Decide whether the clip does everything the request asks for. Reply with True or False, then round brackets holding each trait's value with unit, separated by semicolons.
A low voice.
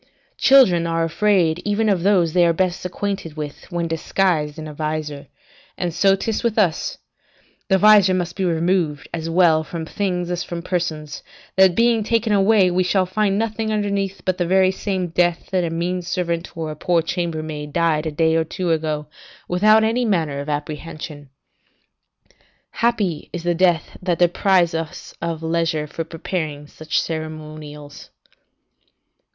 False (175 Hz)